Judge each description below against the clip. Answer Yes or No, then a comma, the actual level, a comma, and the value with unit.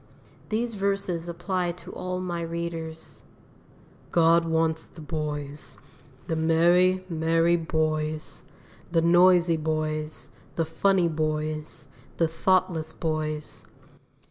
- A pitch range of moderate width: No, narrow, 2.0 semitones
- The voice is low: No, medium, 165 Hz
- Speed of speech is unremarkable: No, slow, 100 wpm